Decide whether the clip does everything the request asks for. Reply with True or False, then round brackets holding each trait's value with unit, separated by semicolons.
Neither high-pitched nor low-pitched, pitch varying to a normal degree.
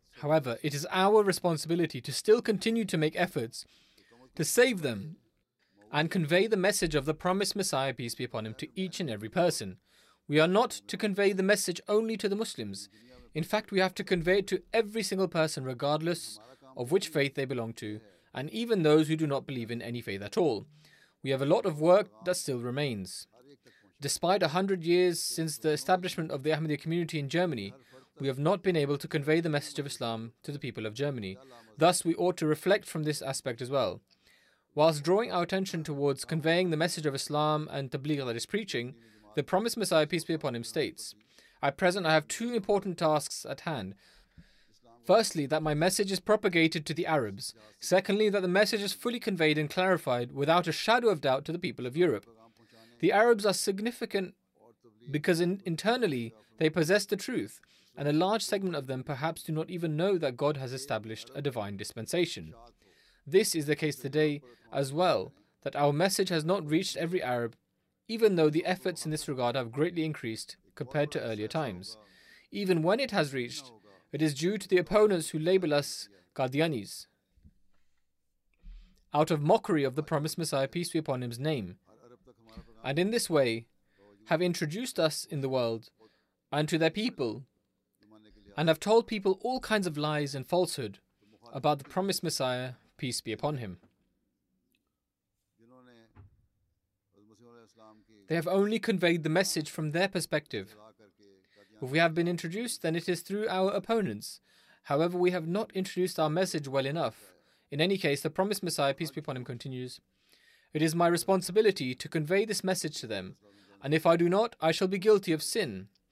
False (155 Hz; 6.5 semitones)